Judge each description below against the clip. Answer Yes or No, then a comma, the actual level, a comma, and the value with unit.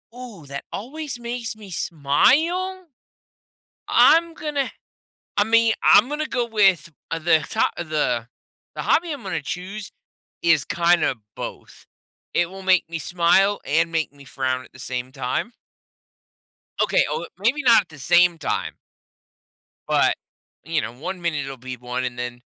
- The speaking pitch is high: No, medium, 175 Hz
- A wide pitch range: Yes, wide, 8.2 semitones